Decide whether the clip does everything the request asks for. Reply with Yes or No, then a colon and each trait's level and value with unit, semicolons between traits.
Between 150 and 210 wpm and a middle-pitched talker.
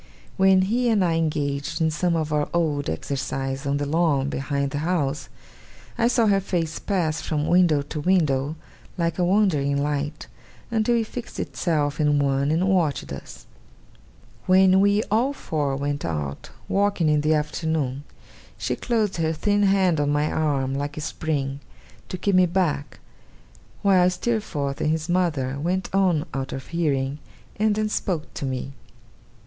Yes: average, 160 wpm; medium, 155 Hz